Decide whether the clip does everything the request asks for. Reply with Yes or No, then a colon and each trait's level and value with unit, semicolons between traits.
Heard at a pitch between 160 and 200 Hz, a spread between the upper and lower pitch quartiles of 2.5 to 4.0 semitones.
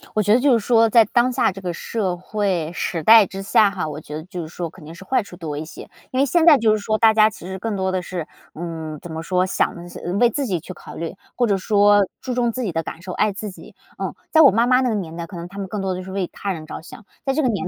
No: high, 195 Hz; average, 4.5 semitones